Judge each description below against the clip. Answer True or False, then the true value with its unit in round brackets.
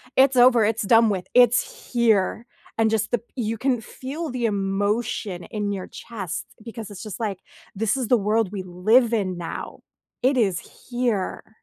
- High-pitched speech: True (220 Hz)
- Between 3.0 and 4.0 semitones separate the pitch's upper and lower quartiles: True (3.3 semitones)